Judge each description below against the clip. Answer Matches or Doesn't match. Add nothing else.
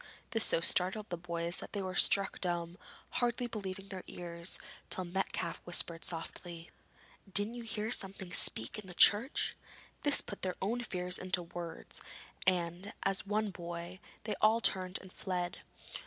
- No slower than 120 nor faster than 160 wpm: Matches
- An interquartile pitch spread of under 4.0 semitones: Matches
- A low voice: Doesn't match